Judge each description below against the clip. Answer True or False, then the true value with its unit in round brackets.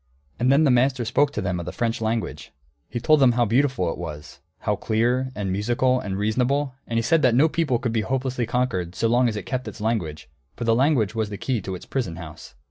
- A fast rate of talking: True (245 wpm)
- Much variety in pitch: False (3.9 semitones)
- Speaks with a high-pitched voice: False (120 Hz)